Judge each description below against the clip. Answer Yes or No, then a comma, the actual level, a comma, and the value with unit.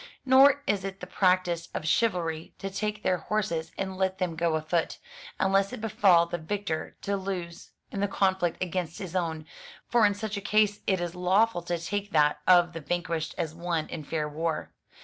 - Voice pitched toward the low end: No, medium, 180 Hz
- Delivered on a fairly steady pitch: No, average, 3.1 semitones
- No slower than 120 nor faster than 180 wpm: No, average, 190 wpm